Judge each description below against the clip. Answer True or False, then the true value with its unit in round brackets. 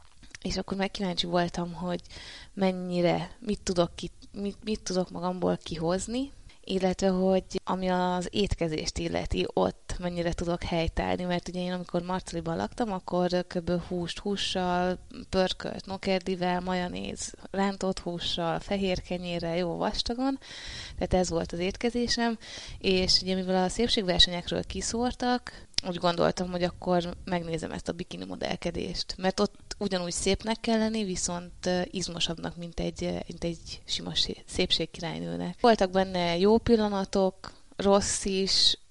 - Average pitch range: False (2.0 semitones)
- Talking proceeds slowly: False (125 wpm)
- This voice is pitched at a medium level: True (180 Hz)